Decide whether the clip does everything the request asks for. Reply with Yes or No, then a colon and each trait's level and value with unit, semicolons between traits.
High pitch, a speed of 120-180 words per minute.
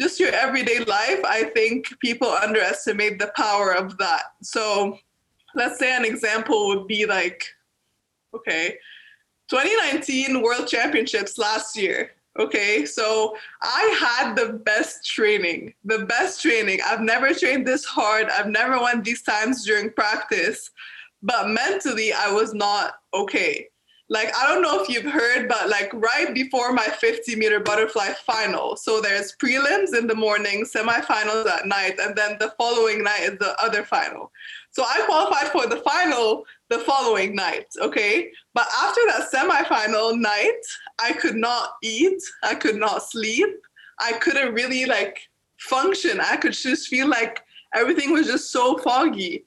Yes: high, 240 Hz; average, 155 wpm